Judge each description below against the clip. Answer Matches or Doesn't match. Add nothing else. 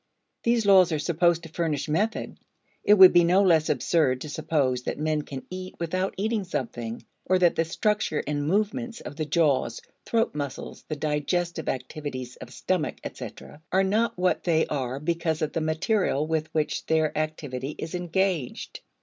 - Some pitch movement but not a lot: Matches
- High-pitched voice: Doesn't match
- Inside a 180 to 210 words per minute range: Doesn't match